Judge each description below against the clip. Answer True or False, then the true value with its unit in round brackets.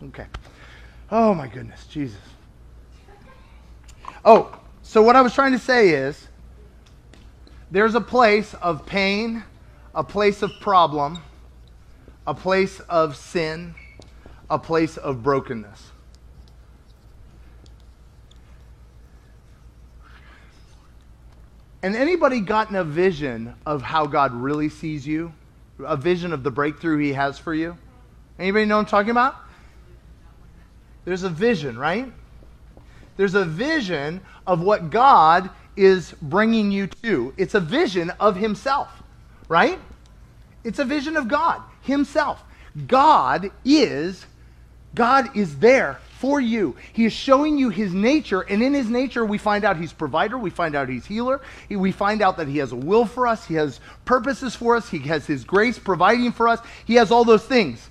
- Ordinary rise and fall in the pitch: False (9.0 semitones)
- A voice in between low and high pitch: True (175 Hz)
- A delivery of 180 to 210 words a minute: False (145 wpm)